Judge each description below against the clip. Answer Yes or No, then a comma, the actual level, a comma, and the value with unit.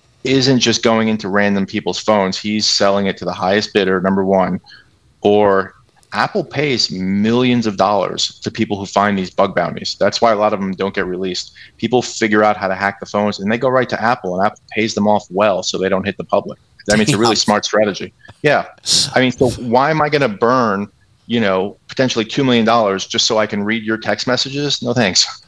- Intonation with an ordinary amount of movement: Yes, average, 3.4 semitones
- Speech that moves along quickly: Yes, fast, 225 wpm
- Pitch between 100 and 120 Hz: Yes, low, 105 Hz